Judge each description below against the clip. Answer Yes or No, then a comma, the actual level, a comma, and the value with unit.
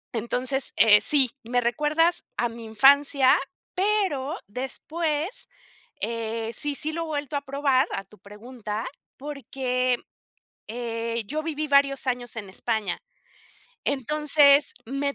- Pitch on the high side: Yes, very high, 265 Hz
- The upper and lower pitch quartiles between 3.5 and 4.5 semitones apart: Yes, average, 4.1 semitones